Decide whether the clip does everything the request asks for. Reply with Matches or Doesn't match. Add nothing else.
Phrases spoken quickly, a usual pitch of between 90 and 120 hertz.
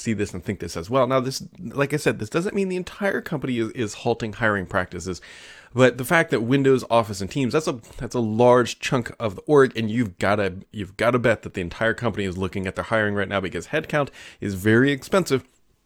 Matches